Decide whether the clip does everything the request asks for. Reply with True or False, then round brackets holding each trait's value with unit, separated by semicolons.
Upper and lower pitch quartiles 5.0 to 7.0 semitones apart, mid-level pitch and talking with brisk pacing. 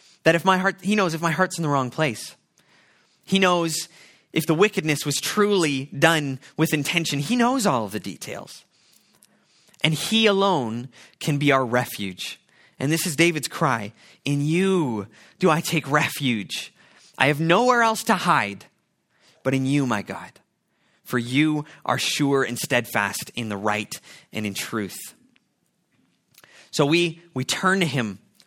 False (5.4 semitones; 150 Hz; 160 wpm)